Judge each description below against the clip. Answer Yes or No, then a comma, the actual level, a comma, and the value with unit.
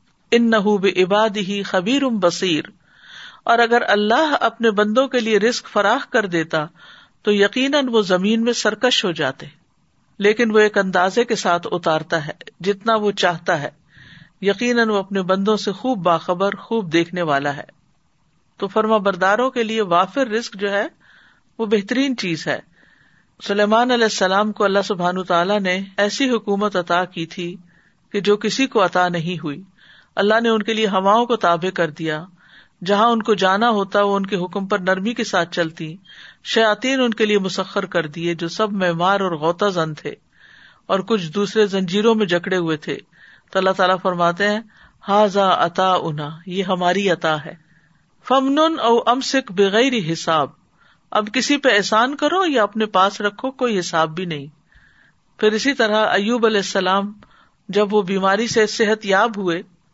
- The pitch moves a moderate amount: Yes, average, 3.8 semitones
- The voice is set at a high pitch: Yes, high, 200 Hz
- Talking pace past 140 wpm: Yes, average, 170 wpm